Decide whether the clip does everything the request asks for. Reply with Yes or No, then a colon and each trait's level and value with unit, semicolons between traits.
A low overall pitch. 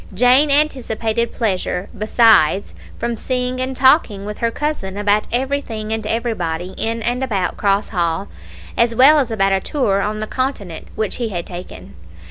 No: high, 220 Hz